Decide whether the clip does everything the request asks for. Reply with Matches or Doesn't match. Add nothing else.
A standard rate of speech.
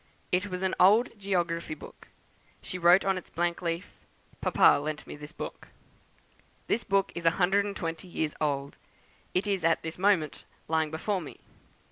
Matches